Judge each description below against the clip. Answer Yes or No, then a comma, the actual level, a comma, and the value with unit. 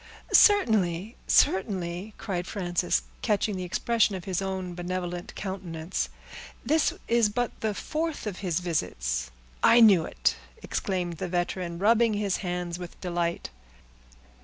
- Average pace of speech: No, slow, 125 wpm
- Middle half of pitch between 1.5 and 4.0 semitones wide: Yes, average, 3.2 semitones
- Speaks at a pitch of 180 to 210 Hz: Yes, medium, 185 Hz